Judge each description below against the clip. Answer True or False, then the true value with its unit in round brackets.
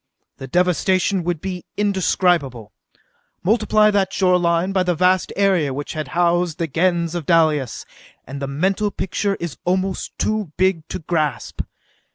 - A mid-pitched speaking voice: True (175 Hz)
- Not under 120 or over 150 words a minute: True (145 wpm)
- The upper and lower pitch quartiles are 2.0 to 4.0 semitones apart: True (3.3 semitones)